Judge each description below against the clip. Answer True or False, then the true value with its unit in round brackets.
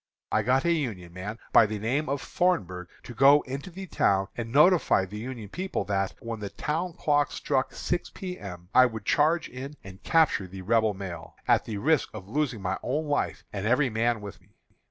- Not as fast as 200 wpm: False (205 wpm)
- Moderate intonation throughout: False (6.7 semitones)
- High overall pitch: False (115 Hz)